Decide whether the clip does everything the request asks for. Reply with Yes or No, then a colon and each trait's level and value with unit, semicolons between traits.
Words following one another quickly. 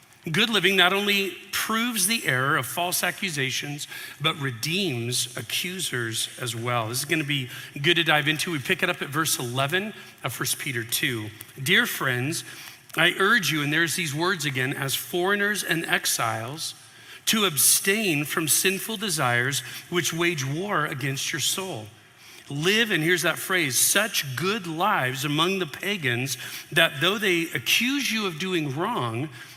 No: average, 160 wpm